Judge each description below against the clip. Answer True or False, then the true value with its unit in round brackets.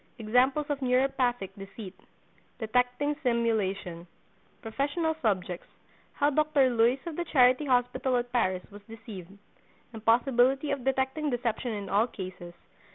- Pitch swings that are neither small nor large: True (4.4 semitones)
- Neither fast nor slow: False (100 wpm)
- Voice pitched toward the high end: True (245 Hz)